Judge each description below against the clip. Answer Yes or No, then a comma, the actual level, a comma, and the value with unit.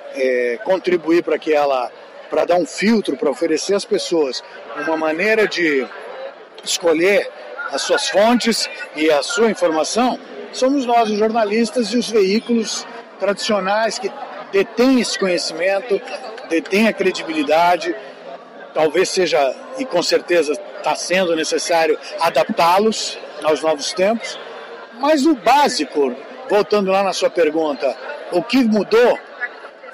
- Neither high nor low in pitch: No, high, 195 Hz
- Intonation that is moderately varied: No, wide, 5.9 semitones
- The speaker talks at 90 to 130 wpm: Yes, slow, 120 wpm